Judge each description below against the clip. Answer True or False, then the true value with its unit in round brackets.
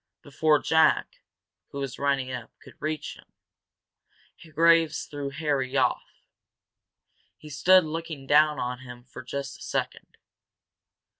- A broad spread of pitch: False (2.7 semitones)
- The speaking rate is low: True (125 wpm)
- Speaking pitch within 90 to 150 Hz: True (140 Hz)